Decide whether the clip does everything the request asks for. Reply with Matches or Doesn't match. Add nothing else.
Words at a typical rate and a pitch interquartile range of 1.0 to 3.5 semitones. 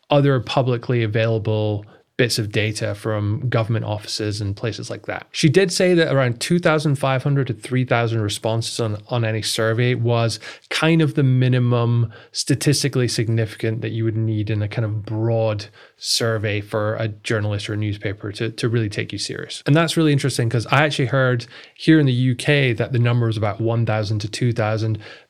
Matches